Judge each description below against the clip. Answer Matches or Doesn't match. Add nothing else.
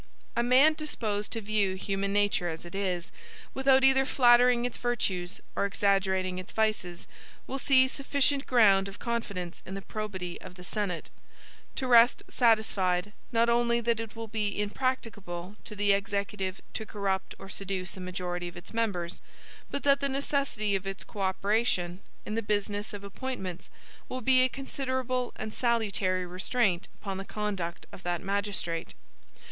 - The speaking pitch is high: Matches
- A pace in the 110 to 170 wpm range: Matches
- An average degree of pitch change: Matches